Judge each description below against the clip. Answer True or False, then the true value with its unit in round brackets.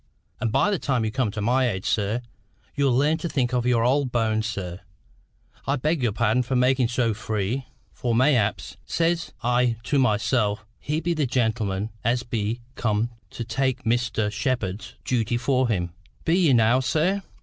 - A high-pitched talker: False (120 Hz)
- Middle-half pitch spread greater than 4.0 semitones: False (3.2 semitones)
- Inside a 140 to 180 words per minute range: True (175 wpm)